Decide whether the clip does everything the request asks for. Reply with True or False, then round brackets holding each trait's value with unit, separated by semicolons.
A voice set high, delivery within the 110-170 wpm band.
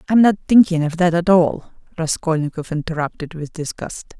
False (170 Hz; 160 wpm)